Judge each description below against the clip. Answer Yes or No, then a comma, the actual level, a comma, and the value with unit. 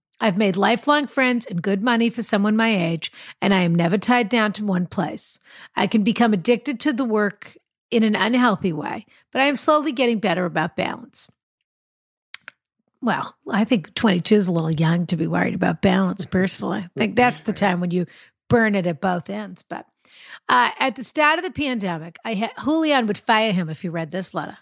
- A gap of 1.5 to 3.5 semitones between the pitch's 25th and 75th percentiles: No, average, 4.8 semitones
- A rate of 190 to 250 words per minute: Yes, fast, 205 wpm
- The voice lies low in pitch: No, high, 215 Hz